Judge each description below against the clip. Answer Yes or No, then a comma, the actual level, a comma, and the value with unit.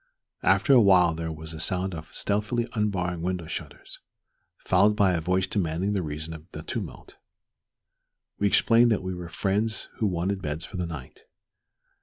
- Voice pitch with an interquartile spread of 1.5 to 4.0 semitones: Yes, average, 3.7 semitones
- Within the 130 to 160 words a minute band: No, average, 170 wpm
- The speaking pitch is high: No, very low, 90 Hz